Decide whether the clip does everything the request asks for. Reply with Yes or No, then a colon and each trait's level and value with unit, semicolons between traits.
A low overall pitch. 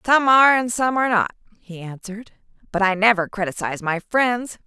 No: high, 215 Hz